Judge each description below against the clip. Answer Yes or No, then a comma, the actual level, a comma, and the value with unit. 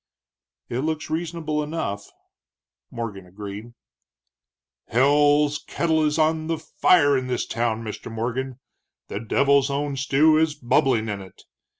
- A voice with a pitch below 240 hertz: Yes, medium, 140 Hz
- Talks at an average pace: No, slow, 125 wpm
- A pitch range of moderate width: Yes, average, 5.0 semitones